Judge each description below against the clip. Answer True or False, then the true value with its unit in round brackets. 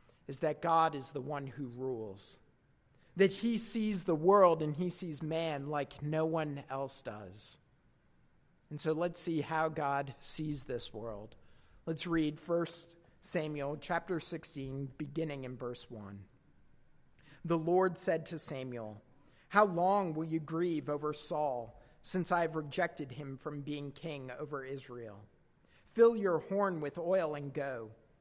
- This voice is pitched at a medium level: True (150 Hz)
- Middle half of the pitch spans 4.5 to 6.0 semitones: False (3.6 semitones)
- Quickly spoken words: False (145 wpm)